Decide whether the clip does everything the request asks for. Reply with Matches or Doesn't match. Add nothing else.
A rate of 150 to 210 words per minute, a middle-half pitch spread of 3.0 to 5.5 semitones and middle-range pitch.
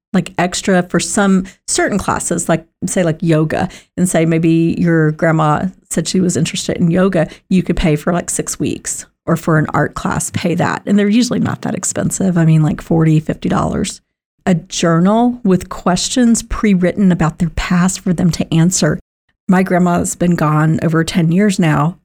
Doesn't match